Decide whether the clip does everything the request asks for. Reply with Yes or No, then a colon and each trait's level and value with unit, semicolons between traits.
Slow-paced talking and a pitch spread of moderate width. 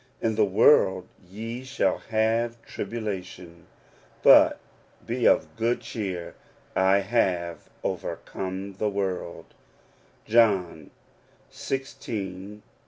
Yes: slow, 90 wpm; average, 3.5 semitones